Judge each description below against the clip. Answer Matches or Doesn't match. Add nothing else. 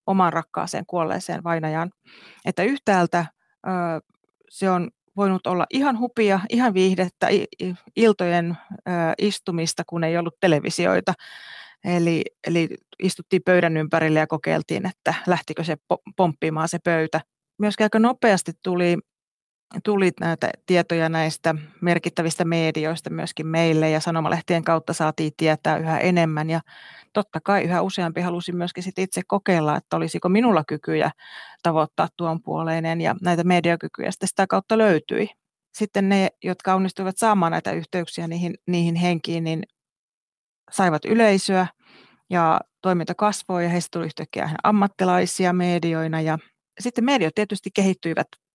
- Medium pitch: Matches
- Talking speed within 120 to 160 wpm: Matches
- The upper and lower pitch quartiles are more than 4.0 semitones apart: Doesn't match